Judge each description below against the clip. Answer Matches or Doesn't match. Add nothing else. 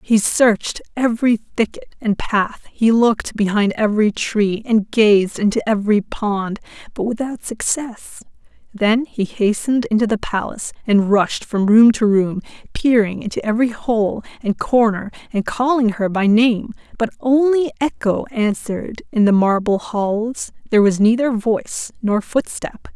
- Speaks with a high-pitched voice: Matches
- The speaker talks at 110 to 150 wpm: Matches